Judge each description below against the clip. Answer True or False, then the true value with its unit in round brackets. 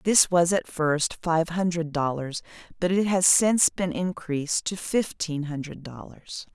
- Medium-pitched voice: True (165 Hz)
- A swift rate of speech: False (155 wpm)